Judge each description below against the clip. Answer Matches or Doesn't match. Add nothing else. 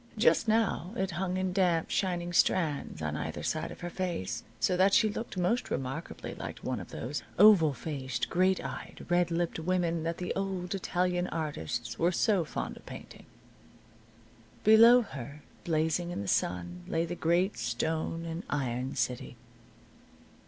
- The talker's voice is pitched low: Doesn't match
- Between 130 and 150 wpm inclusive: Doesn't match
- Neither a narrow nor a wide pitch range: Matches